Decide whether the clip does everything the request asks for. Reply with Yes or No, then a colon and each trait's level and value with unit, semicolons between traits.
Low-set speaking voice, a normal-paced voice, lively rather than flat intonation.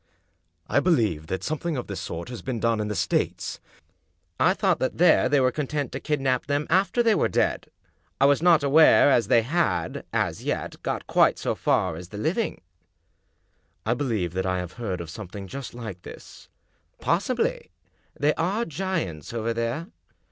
Yes: low, 120 Hz; average, 190 wpm; wide, 8.6 semitones